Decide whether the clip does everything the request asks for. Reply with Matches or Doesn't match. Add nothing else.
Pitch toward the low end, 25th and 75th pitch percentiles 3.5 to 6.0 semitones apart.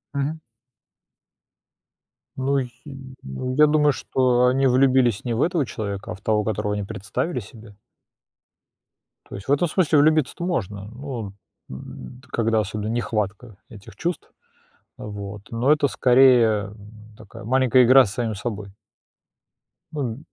Matches